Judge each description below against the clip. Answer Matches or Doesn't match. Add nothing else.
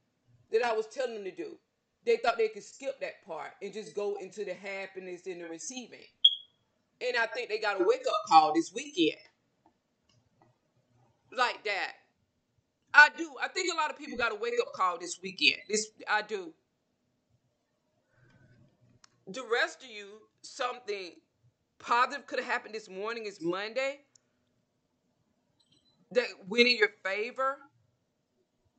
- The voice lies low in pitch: Doesn't match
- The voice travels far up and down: Matches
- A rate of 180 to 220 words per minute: Doesn't match